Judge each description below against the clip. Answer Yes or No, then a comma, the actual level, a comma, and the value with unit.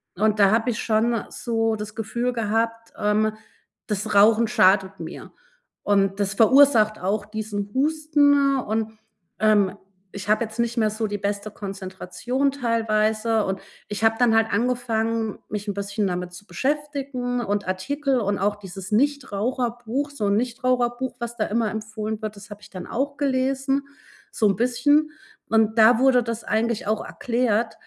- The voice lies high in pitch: Yes, high, 220 Hz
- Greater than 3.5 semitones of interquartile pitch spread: No, average, 3.1 semitones